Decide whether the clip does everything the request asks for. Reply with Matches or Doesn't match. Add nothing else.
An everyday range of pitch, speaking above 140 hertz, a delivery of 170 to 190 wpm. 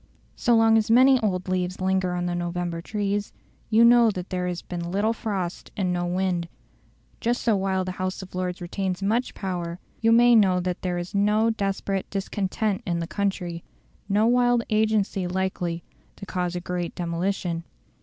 Matches